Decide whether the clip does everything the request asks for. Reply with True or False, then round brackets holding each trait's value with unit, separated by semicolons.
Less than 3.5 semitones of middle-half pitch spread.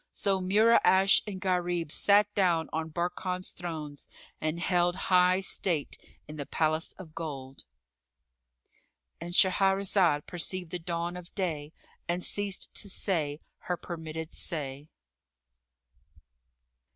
True (2.9 semitones)